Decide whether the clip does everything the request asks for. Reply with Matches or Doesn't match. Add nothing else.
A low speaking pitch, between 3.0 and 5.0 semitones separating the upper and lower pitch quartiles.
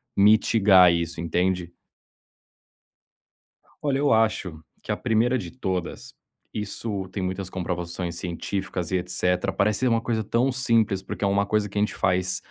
Matches